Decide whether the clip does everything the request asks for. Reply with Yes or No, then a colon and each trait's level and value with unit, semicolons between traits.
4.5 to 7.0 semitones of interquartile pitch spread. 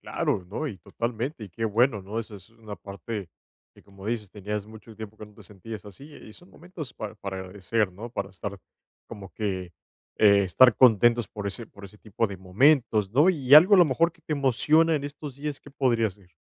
Yes: average, 4.8 semitones